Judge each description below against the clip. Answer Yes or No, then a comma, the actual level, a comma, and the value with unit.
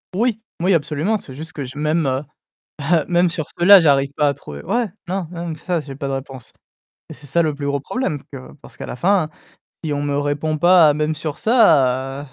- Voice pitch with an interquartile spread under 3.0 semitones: No, average, 3.6 semitones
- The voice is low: No, medium, 150 Hz